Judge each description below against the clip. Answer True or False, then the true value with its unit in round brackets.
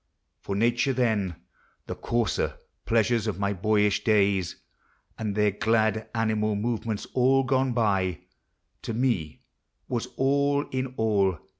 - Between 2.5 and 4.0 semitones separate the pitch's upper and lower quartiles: True (3.0 semitones)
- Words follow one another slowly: True (120 wpm)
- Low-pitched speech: True (110 Hz)